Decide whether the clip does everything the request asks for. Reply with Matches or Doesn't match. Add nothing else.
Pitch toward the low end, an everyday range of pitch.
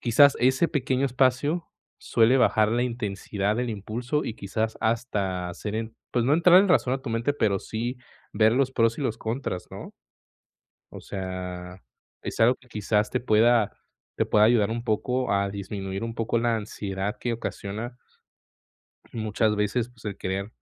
Matches